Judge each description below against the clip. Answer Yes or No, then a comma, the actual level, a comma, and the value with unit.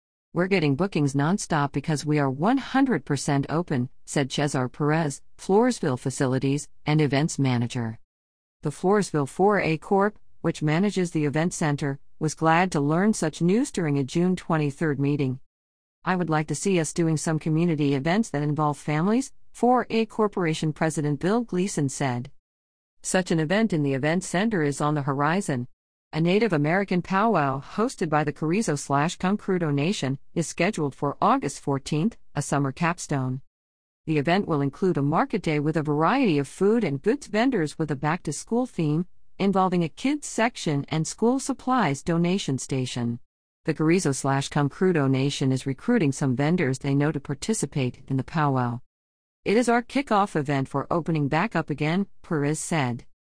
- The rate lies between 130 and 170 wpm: Yes, average, 160 wpm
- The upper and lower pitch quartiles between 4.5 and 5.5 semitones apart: Yes, average, 4.8 semitones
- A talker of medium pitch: Yes, medium, 155 Hz